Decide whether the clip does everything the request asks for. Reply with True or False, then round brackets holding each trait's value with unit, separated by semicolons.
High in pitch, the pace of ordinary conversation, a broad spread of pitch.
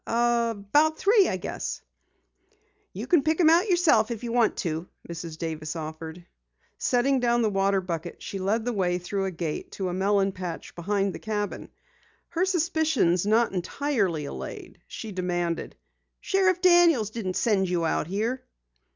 True (205 Hz; 160 wpm; 6.3 semitones)